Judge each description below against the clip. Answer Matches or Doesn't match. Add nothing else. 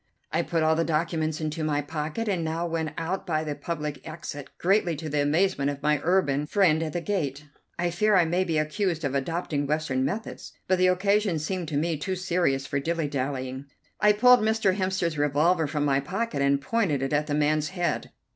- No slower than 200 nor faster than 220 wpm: Matches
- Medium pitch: Matches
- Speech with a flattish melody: Doesn't match